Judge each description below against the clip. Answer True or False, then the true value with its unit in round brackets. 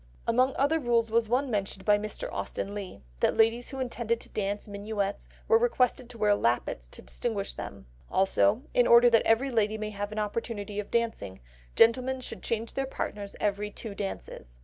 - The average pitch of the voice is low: False (220 Hz)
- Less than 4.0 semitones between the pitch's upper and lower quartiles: True (3.0 semitones)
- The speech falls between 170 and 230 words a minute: True (185 wpm)